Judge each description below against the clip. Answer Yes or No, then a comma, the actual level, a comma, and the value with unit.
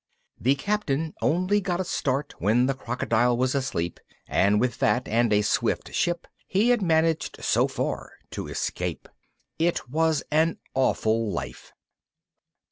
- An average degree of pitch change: No, wide, 5.7 semitones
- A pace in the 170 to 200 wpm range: No, average, 140 wpm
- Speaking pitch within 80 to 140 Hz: Yes, low, 135 Hz